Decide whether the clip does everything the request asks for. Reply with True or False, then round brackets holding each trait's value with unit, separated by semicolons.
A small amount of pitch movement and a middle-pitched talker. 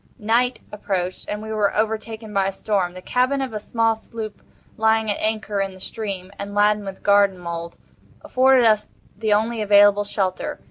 False (2.0 semitones; 210 Hz)